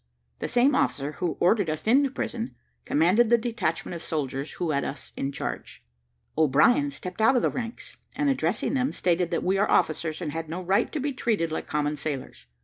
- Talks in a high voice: No, medium, 180 Hz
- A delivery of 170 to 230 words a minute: Yes, average, 200 wpm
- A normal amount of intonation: No, wide, 7.4 semitones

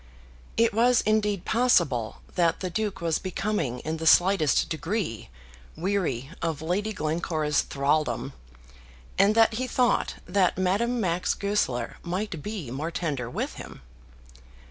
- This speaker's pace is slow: Yes, slow, 130 wpm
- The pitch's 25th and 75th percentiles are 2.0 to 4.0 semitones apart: No, average, 5.2 semitones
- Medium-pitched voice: Yes, medium, 180 Hz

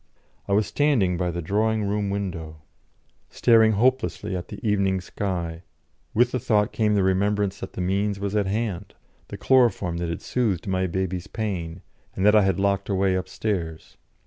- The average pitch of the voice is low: Yes, low, 100 Hz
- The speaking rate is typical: Yes, average, 170 wpm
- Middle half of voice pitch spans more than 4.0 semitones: No, narrow, 2.5 semitones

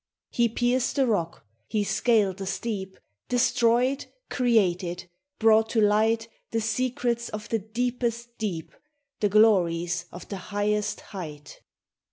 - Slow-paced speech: Yes, slow, 125 wpm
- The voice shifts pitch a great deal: No, average, 3.6 semitones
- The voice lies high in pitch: Yes, high, 220 Hz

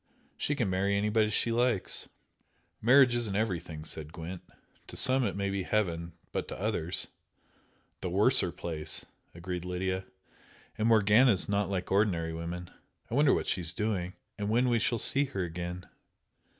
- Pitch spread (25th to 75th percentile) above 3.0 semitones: Yes, average, 4.0 semitones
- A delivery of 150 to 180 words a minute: Yes, average, 165 wpm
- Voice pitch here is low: Yes, low, 100 Hz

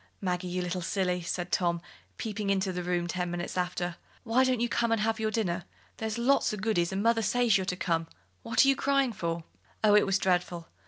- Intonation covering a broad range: No, average, 4.1 semitones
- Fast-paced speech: Yes, fast, 220 wpm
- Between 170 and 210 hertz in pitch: Yes, high, 190 Hz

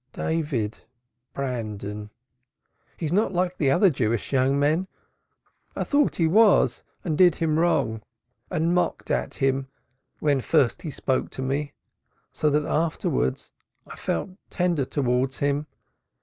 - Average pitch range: Yes, average, 4.4 semitones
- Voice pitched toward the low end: No, medium, 145 Hz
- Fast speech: No, slow, 135 wpm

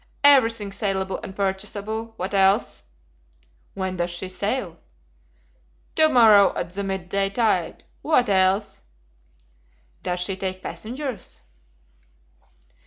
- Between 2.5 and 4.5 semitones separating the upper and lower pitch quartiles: Yes, average, 2.8 semitones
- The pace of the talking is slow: Yes, slow, 105 wpm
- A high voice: Yes, high, 195 Hz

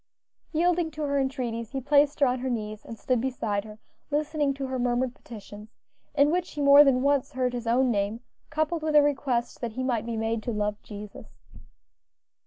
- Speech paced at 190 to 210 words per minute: Yes, average, 195 wpm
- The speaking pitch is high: Yes, very high, 255 Hz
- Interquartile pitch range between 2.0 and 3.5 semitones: No, average, 4.0 semitones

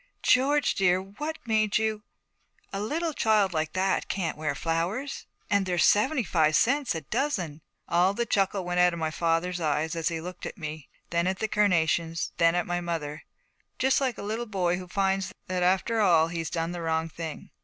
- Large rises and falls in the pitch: No, average, 4.3 semitones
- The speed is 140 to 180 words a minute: No, average, 190 wpm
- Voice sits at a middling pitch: Yes, medium, 180 Hz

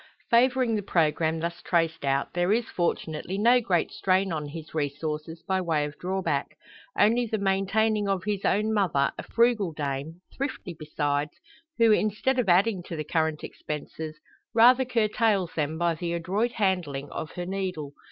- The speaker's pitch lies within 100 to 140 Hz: No, medium, 180 Hz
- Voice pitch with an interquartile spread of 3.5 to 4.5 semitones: No, average, 5.1 semitones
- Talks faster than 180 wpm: No, average, 160 wpm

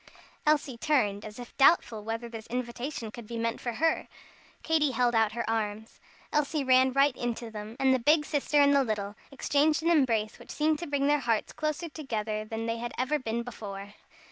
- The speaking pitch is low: No, high, 245 Hz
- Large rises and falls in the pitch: No, average, 4.5 semitones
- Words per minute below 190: No, average, 195 wpm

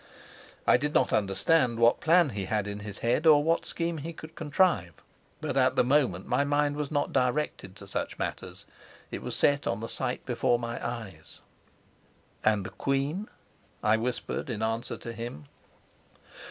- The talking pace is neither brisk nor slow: Yes, average, 170 wpm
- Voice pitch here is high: No, low, 125 Hz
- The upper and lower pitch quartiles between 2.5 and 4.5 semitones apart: No, average, 5.3 semitones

